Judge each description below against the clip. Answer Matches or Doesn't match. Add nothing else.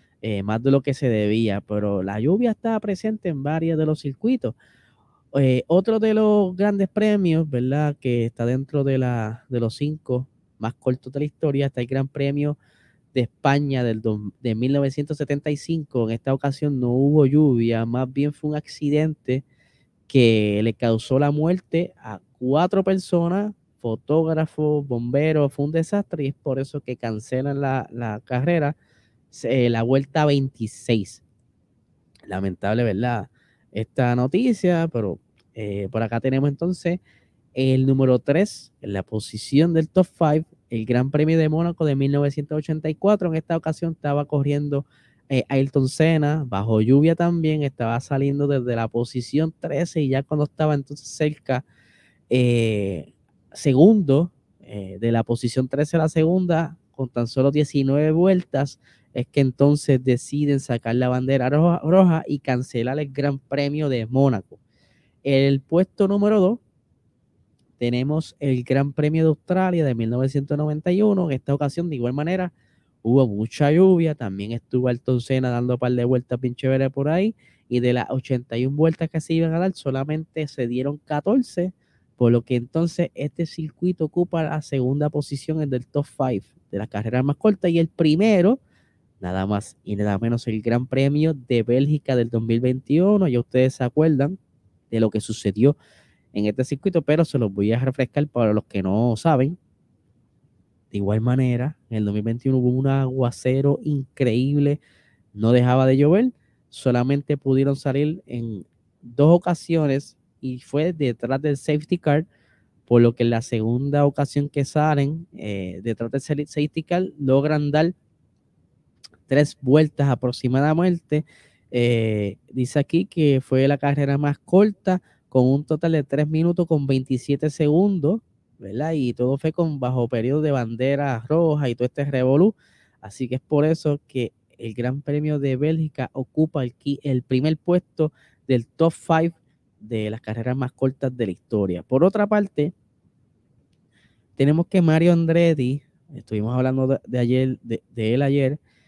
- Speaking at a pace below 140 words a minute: Doesn't match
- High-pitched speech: Doesn't match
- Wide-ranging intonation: Doesn't match